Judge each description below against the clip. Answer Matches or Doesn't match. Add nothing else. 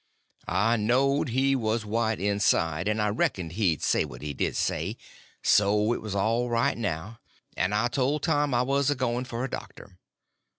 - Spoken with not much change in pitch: Doesn't match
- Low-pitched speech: Matches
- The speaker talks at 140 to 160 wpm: Doesn't match